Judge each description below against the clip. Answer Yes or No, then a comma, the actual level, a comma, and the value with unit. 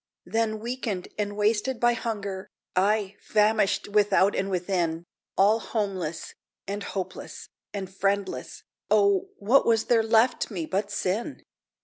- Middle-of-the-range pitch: No, high, 205 Hz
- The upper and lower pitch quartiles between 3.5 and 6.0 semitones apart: No, average, 2.7 semitones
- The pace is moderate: No, slow, 125 wpm